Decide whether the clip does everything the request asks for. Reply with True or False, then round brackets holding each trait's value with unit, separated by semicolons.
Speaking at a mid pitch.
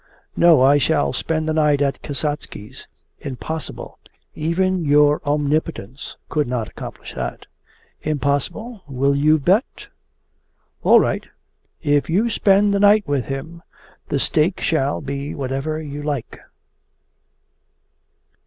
True (150 Hz)